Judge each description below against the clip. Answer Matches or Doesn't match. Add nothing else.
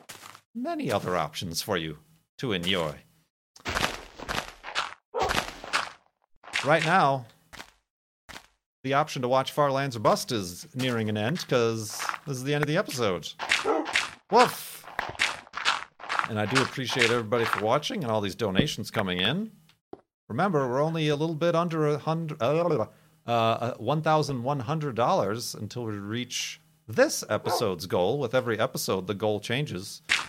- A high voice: Doesn't match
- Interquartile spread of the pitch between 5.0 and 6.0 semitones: Matches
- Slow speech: Matches